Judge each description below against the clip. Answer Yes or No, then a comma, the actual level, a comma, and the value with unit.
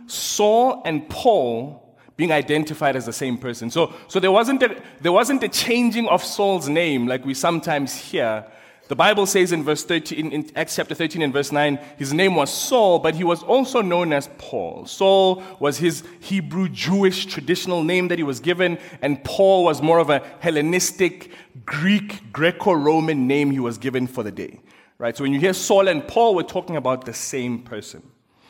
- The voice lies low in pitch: No, medium, 165 Hz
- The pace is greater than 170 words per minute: Yes, average, 190 wpm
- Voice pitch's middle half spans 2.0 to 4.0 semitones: No, average, 4.8 semitones